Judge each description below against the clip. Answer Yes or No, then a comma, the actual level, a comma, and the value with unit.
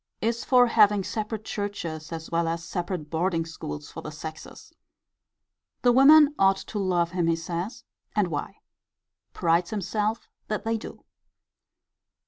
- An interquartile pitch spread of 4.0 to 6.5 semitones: Yes, average, 4.6 semitones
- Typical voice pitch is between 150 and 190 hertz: Yes, medium, 185 Hz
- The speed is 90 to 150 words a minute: Yes, average, 140 wpm